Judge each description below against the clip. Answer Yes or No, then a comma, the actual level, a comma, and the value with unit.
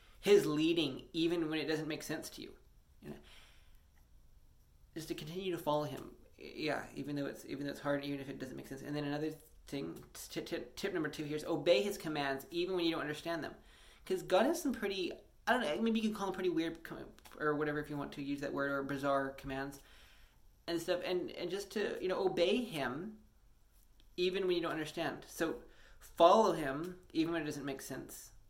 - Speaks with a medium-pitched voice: Yes, medium, 150 Hz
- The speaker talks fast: Yes, fast, 215 wpm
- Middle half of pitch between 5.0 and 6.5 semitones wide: No, average, 4.2 semitones